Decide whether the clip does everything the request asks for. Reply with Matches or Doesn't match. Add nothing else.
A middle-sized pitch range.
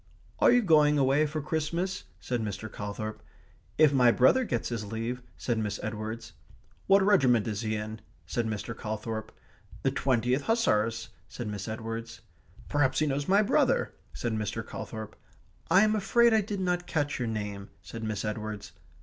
Doesn't match